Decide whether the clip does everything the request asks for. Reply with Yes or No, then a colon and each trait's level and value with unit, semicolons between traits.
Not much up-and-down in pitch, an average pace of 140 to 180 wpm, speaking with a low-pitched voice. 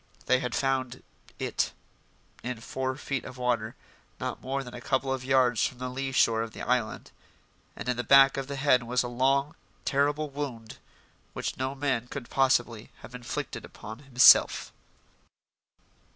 Yes: narrow, 1.9 semitones; average, 165 wpm; low, 130 Hz